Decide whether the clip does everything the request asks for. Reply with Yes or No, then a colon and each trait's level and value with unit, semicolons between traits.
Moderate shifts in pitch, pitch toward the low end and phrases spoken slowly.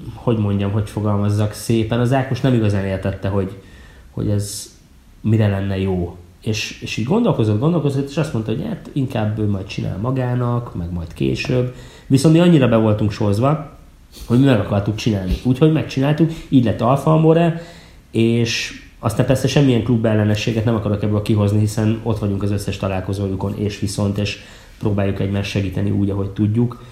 No: average, 3.8 semitones; low, 105 Hz; average, 165 wpm